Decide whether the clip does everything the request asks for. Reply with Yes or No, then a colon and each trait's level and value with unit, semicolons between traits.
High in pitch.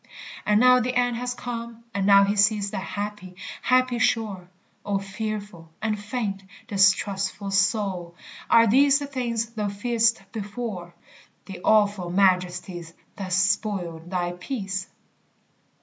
Yes: high, 205 Hz